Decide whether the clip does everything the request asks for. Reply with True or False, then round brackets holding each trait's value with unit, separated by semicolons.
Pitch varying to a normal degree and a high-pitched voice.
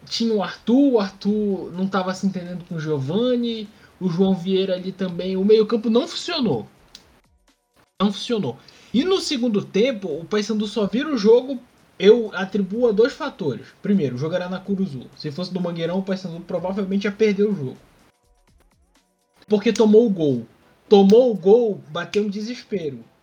True (3.5 semitones; 205 Hz)